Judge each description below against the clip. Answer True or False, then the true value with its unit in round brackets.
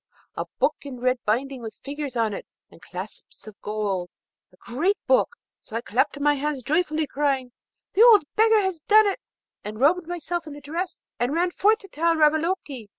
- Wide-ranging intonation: True (5.9 semitones)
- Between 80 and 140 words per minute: False (190 wpm)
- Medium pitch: False (295 Hz)